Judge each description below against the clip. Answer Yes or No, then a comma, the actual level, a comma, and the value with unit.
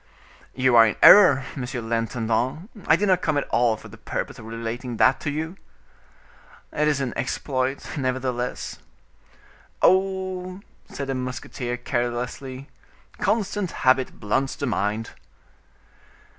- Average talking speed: No, slow, 130 wpm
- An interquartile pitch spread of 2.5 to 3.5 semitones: No, average, 4.0 semitones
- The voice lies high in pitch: No, low, 130 Hz